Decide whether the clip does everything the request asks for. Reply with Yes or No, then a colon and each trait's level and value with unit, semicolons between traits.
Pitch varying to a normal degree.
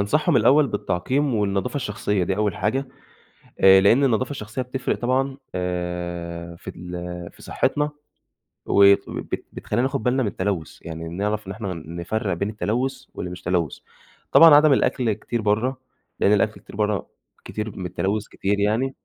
No: wide, 6.1 semitones